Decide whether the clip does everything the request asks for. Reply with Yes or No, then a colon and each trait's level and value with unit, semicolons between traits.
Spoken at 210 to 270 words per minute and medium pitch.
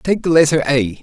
Yes: fast, 235 wpm; medium, 145 Hz